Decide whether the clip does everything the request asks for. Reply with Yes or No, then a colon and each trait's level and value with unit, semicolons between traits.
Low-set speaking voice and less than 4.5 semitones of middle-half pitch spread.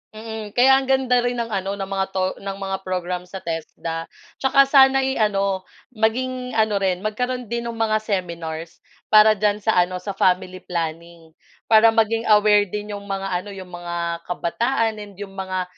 No: high, 205 Hz; average, 3.7 semitones